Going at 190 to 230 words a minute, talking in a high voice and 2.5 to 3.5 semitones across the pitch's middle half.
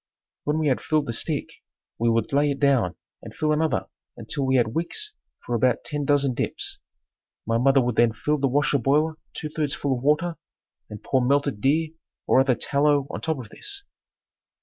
No: average, 195 wpm; medium, 140 Hz; average, 3.2 semitones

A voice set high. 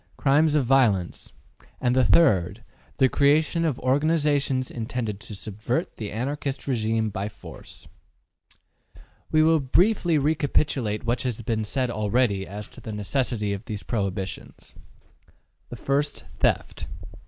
No: low, 125 Hz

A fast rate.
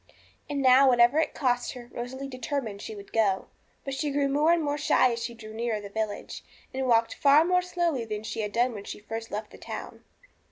Yes: fast, 220 wpm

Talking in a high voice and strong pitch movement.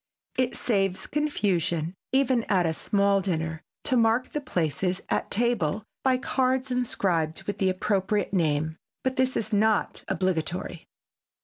Yes: high, 200 Hz; wide, 6.2 semitones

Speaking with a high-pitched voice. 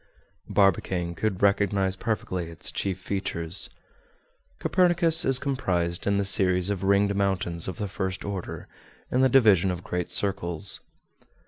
No: very low, 95 Hz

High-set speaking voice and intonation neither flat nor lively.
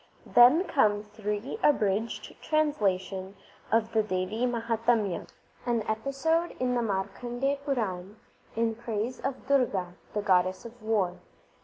Yes: high, 225 Hz; average, 3.7 semitones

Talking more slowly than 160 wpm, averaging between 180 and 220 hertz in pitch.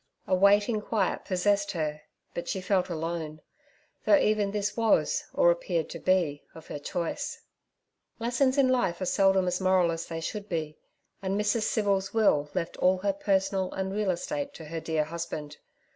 No: average, 175 wpm; high, 190 Hz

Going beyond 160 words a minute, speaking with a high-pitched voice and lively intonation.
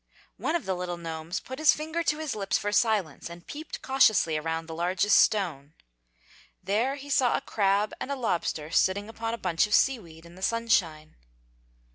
Yes: average, 190 wpm; high, 200 Hz; wide, 6.1 semitones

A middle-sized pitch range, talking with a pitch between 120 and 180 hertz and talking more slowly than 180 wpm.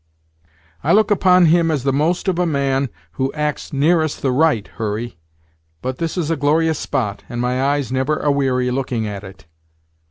No: average, 4.1 semitones; medium, 140 Hz; average, 185 wpm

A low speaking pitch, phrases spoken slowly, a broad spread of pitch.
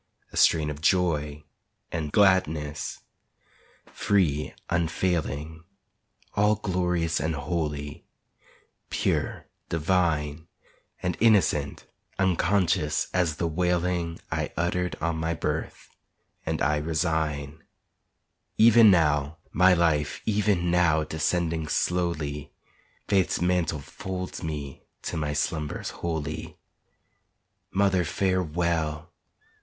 No: very low, 80 Hz; slow, 95 wpm; average, 2.9 semitones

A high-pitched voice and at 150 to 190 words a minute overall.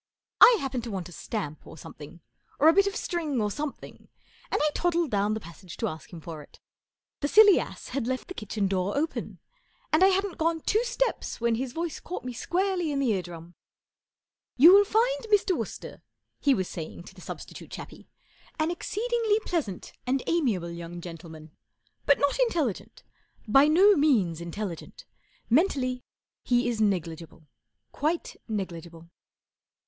Yes: very high, 255 Hz; average, 170 wpm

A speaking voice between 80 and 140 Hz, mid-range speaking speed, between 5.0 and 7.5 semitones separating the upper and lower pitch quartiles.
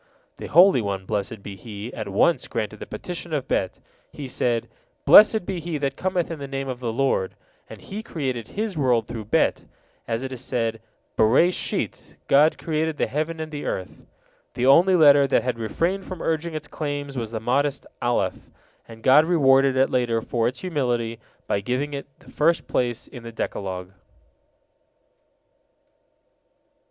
Yes: low, 135 Hz; average, 170 wpm; wide, 5.4 semitones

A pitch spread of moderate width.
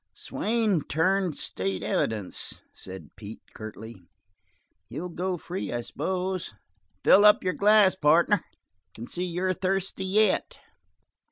No: wide, 8.2 semitones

